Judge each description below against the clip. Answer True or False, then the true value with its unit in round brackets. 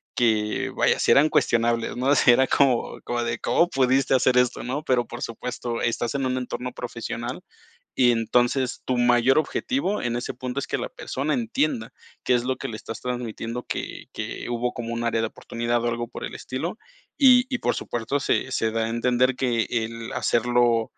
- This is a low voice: True (120 Hz)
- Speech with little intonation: True (1.8 semitones)